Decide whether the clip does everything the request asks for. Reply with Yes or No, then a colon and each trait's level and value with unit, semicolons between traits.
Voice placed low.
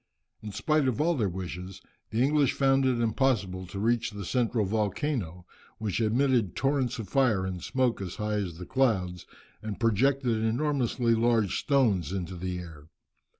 Yes: low, 110 Hz